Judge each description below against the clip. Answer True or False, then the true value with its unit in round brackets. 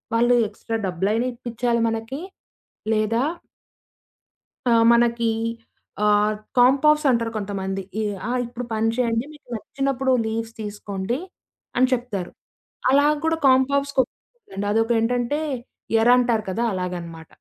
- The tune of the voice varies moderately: True (3.0 semitones)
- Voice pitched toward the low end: False (230 Hz)